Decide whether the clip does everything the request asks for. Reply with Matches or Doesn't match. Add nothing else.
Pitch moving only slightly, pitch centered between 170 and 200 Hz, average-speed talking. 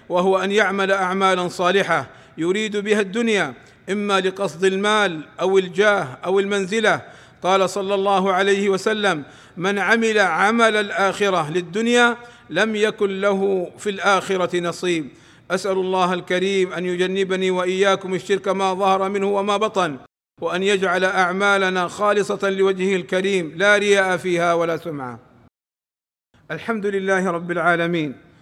Matches